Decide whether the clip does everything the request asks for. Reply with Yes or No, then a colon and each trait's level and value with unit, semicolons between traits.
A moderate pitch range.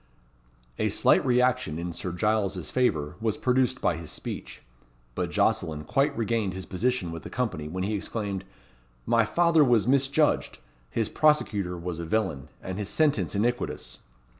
No: wide, 6.1 semitones